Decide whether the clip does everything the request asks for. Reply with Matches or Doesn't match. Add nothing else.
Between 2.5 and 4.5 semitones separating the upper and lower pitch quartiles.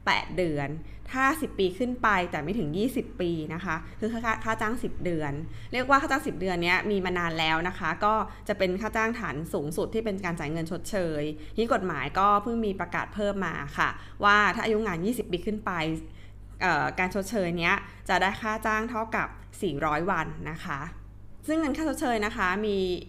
Doesn't match